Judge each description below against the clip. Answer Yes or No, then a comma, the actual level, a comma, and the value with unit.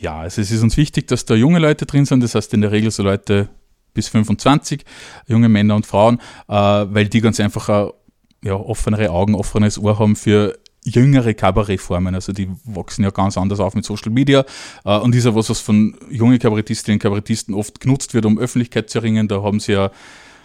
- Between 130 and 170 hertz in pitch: No, low, 110 Hz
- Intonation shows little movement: Yes, narrow, 2.3 semitones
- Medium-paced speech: No, fast, 205 wpm